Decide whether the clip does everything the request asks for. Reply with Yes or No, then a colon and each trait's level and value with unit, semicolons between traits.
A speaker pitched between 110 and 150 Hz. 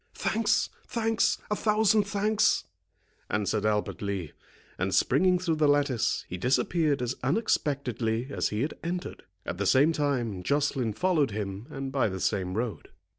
Yes: low, 135 Hz